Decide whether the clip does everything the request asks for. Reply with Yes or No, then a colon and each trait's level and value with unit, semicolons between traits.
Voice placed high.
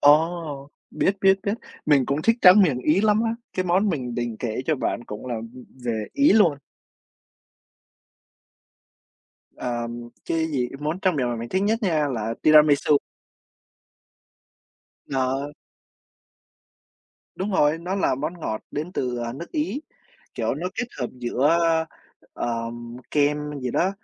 No: medium, 150 Hz